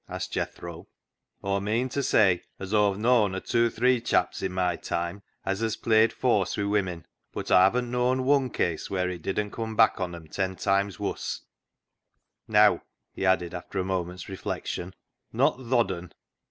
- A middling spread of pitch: Yes, average, 3.8 semitones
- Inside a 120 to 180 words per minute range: No, average, 195 wpm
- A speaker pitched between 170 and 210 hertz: No, low, 100 Hz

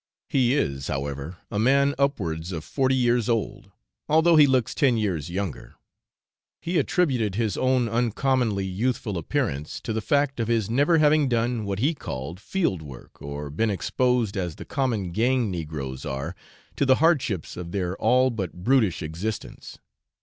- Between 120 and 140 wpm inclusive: No, average, 160 wpm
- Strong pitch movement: Yes, wide, 6.9 semitones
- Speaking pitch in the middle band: No, low, 110 Hz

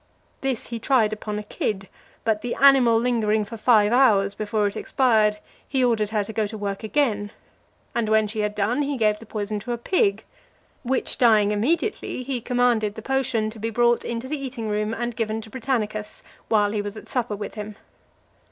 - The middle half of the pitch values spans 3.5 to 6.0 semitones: No, average, 2.7 semitones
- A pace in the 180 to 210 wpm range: Yes, average, 200 wpm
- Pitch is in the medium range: No, high, 220 Hz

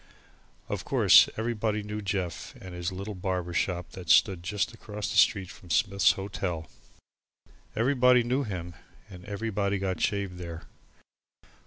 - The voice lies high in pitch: No, low, 100 Hz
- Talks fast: No, average, 140 wpm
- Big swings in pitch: No, average, 3.0 semitones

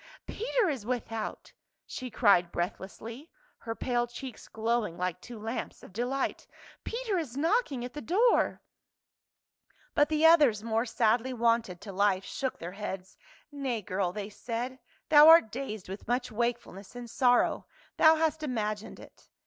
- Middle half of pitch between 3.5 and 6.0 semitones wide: Yes, average, 4.6 semitones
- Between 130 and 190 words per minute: Yes, average, 160 wpm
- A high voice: Yes, high, 240 Hz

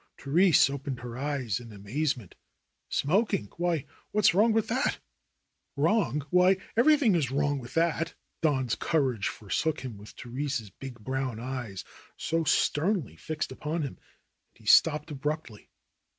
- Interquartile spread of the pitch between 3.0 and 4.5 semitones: No, average, 5.0 semitones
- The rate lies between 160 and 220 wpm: No, average, 140 wpm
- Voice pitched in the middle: Yes, medium, 145 Hz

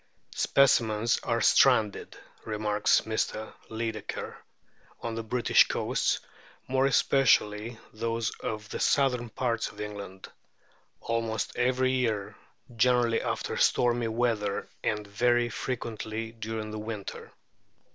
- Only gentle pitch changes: Yes, narrow, 2.0 semitones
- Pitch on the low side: Yes, low, 115 Hz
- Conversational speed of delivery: No, slow, 110 wpm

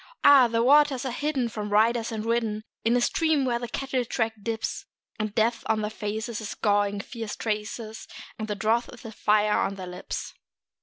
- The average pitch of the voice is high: Yes, high, 225 Hz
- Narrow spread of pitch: Yes, narrow, 2.2 semitones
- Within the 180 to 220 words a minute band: Yes, average, 195 wpm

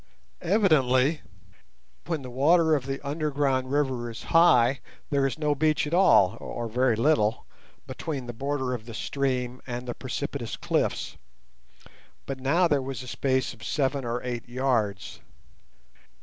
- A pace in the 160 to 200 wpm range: No, average, 150 wpm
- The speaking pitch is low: Yes, low, 130 Hz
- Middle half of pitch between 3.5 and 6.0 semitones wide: No, average, 3.0 semitones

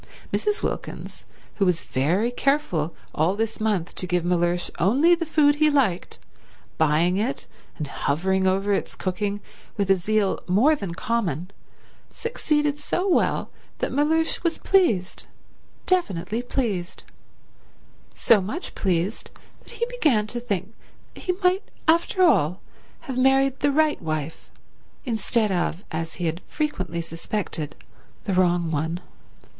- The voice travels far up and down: Yes, wide, 8.5 semitones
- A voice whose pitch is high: Yes, high, 205 Hz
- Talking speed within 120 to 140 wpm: Yes, slow, 135 wpm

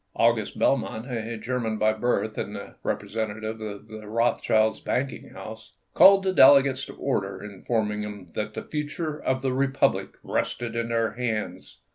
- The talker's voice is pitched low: Yes, low, 115 Hz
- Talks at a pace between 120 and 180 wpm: Yes, average, 155 wpm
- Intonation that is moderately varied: Yes, average, 3.2 semitones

